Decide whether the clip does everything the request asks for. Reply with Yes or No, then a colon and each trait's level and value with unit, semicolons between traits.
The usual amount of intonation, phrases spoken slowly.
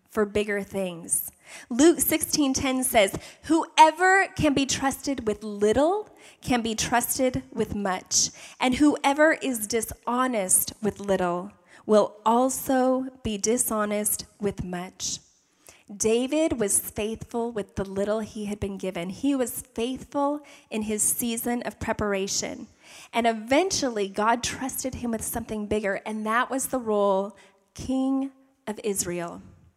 Yes: average, 4.4 semitones; slow, 125 wpm